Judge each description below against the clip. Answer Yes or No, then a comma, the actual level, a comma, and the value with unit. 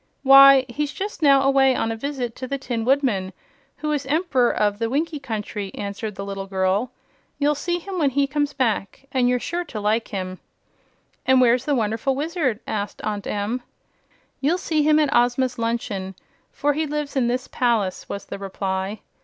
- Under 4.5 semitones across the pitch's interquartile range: No, average, 5.3 semitones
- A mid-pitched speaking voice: No, very high, 255 Hz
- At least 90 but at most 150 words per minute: No, average, 185 wpm